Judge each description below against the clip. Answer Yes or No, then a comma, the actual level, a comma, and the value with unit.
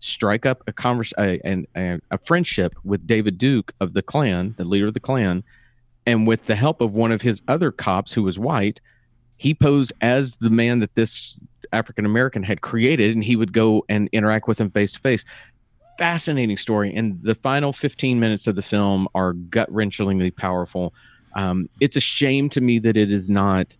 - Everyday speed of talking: Yes, average, 195 wpm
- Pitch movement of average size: Yes, average, 3.5 semitones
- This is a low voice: Yes, low, 110 Hz